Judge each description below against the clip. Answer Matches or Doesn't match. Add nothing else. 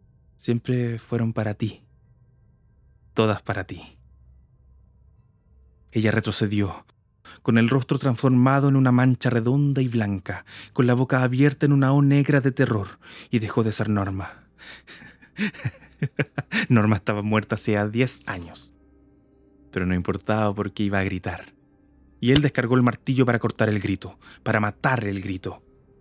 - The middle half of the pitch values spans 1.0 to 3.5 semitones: Doesn't match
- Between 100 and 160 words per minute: Matches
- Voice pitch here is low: Matches